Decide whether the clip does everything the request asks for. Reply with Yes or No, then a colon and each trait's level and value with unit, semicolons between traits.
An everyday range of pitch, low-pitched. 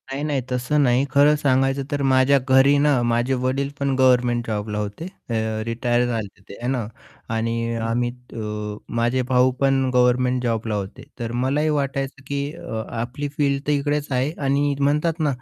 Yes: average, 3.0 semitones; low, 130 Hz